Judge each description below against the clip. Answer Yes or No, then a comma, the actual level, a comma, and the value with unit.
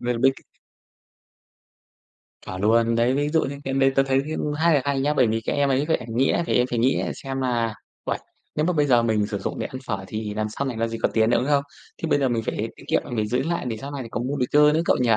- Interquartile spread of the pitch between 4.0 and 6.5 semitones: No, average, 3.6 semitones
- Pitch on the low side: Yes, low, 130 Hz